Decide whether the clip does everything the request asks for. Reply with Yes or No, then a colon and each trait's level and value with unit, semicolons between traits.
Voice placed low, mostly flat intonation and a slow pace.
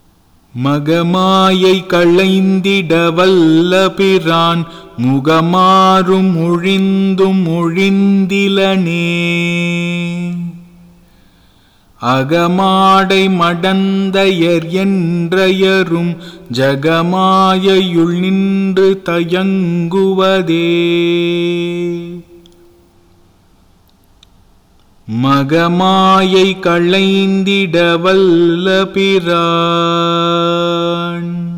No: medium, 175 Hz; narrow, 2.0 semitones; slow, 30 wpm